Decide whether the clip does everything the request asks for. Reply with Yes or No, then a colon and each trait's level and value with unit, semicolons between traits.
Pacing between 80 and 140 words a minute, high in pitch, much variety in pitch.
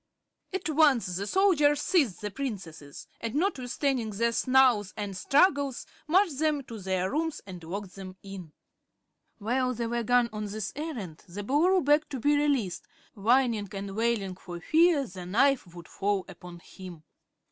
No: average, 160 wpm; high, 230 Hz; wide, 6.7 semitones